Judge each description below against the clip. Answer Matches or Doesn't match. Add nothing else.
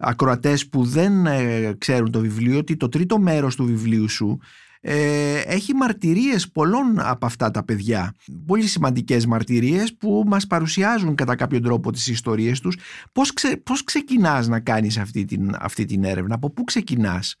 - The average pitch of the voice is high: Doesn't match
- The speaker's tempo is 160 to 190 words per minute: Matches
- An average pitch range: Doesn't match